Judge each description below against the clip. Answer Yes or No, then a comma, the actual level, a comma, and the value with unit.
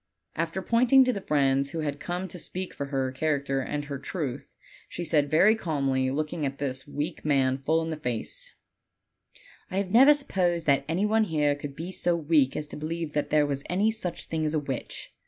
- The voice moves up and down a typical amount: Yes, average, 4.0 semitones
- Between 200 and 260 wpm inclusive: Yes, fast, 205 wpm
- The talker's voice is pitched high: No, medium, 155 Hz